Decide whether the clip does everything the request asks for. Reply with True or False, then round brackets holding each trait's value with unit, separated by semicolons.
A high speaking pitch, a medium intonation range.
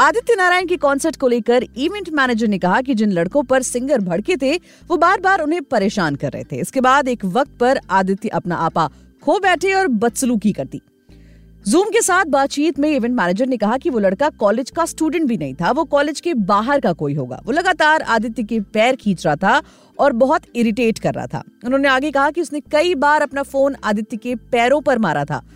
False (255 Hz; 6.7 semitones)